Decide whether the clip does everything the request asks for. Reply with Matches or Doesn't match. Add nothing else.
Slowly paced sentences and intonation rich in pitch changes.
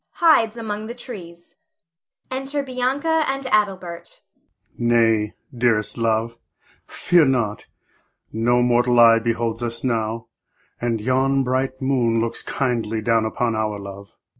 Matches